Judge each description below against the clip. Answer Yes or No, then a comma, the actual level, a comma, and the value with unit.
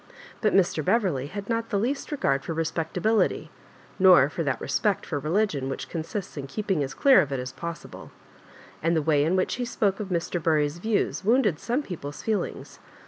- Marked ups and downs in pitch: Yes, wide, 5.9 semitones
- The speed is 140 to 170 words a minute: No, average, 190 wpm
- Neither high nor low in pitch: Yes, medium, 175 Hz